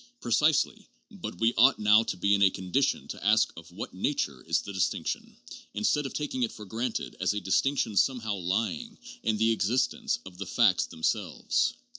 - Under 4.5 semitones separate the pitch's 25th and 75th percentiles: No, average, 4.9 semitones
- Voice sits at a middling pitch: No, low, 110 Hz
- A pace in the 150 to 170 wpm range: No, average, 185 wpm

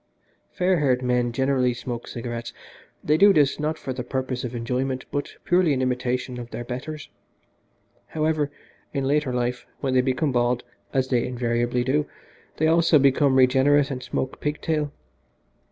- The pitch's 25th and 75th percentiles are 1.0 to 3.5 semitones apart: Yes, average, 2.9 semitones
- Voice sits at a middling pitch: No, low, 130 Hz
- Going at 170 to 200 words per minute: No, average, 160 wpm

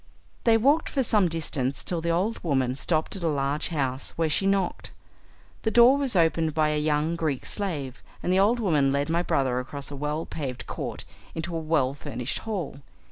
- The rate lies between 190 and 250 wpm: Yes, average, 195 wpm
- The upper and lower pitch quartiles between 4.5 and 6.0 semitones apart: Yes, average, 5.0 semitones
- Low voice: No, medium, 160 Hz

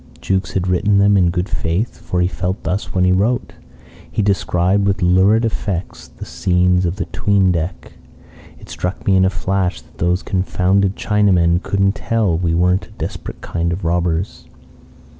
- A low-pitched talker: Yes, very low, 90 Hz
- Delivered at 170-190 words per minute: Yes, average, 180 wpm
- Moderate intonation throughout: No, narrow, 2.0 semitones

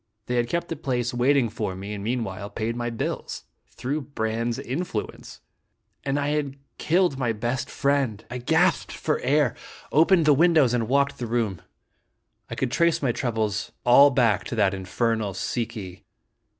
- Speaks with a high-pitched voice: No, low, 120 Hz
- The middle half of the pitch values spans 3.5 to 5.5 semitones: Yes, average, 4.1 semitones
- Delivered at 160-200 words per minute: Yes, average, 165 wpm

